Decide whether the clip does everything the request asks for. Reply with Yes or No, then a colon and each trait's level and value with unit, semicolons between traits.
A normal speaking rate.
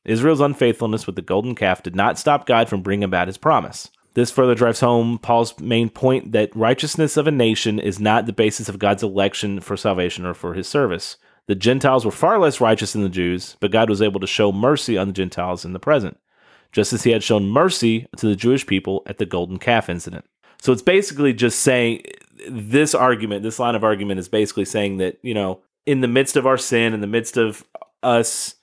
No: fast, 220 wpm